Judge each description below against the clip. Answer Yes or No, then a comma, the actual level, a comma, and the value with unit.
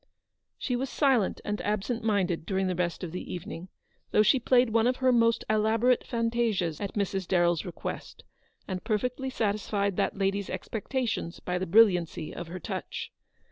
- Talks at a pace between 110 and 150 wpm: No, average, 165 wpm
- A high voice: Yes, high, 205 Hz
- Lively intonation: No, average, 4.2 semitones